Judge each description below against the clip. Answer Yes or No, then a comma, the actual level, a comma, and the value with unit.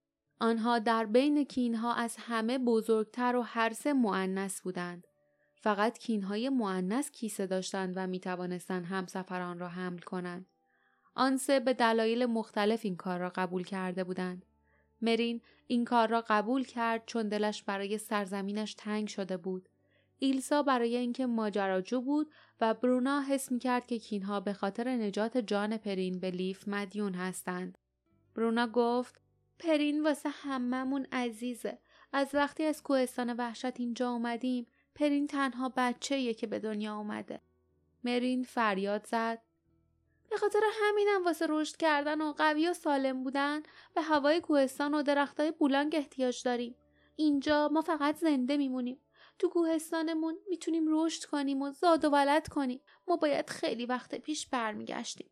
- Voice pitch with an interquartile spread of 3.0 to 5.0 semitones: No, wide, 5.4 semitones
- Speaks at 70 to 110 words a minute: No, average, 145 wpm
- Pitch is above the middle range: Yes, high, 245 Hz